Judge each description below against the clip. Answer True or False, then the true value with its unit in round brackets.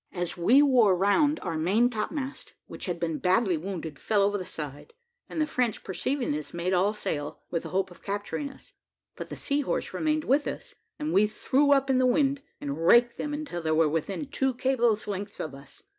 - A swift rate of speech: True (210 wpm)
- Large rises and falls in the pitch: True (7.7 semitones)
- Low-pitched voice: False (205 Hz)